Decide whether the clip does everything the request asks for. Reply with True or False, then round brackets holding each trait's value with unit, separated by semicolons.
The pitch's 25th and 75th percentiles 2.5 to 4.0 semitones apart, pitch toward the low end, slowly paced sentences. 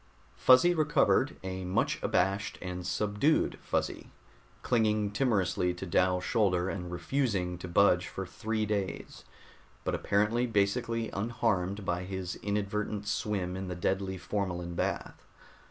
True (3.0 semitones; 100 Hz; 125 wpm)